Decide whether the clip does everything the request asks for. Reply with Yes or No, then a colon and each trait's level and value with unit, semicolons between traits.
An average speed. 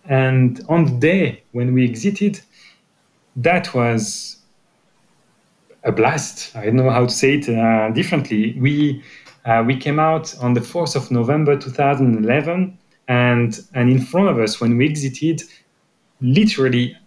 Yes: average, 145 wpm